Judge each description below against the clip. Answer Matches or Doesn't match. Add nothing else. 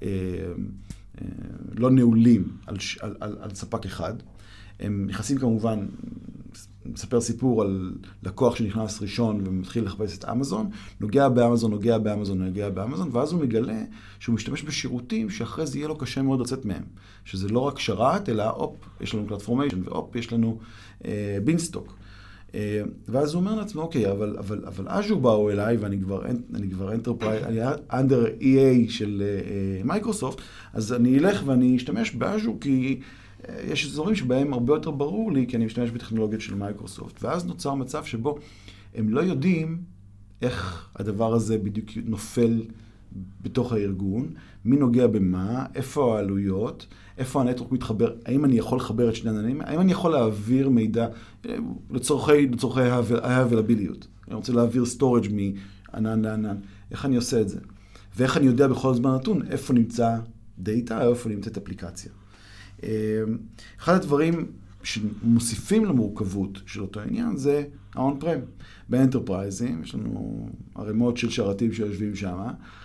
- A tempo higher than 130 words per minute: Matches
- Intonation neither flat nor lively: Matches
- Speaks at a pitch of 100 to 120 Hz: Matches